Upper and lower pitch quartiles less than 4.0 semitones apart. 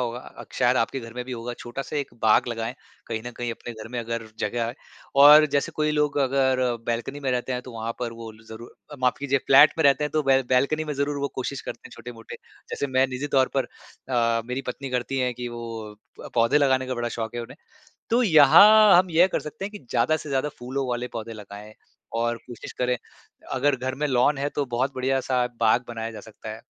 Yes: average, 3.0 semitones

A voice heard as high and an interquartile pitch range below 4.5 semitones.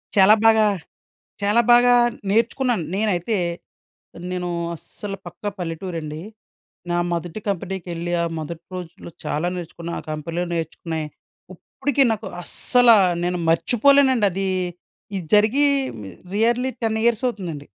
No: high, 195 Hz; average, 5.1 semitones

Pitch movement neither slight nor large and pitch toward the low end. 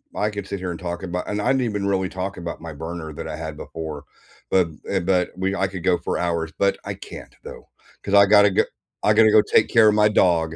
Yes: average, 3.3 semitones; very low, 95 Hz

